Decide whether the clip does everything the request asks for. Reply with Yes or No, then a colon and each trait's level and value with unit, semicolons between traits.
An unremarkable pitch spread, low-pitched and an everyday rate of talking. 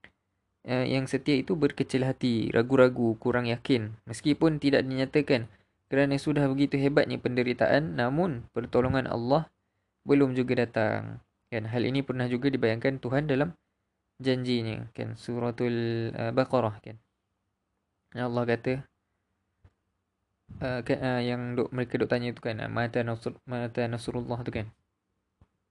Yes: average, 3.0 semitones; low, 120 Hz; average, 130 wpm